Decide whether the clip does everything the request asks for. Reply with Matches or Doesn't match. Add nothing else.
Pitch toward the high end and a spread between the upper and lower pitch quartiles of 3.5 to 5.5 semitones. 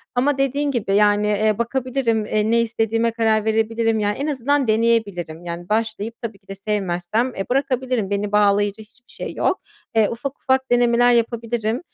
Doesn't match